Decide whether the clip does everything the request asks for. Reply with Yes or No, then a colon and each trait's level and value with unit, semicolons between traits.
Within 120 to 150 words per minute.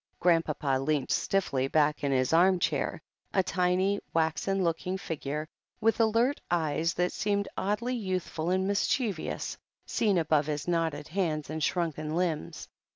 Yes: average, 140 wpm